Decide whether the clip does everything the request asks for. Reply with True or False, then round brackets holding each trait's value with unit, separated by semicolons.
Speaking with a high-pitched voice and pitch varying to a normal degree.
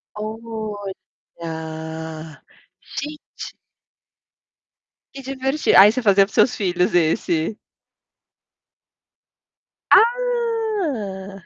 False (205 Hz; 7.5 semitones)